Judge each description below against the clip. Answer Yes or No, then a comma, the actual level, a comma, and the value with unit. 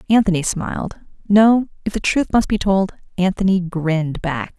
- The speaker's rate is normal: Yes, average, 155 wpm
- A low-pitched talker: No, high, 190 Hz